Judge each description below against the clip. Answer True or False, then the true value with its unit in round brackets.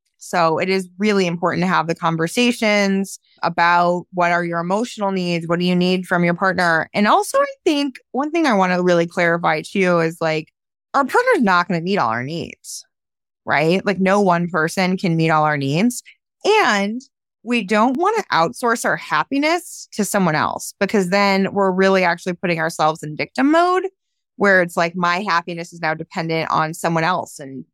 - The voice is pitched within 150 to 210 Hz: True (185 Hz)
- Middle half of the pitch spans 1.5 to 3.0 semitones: False (3.8 semitones)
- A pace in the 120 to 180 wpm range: False (195 wpm)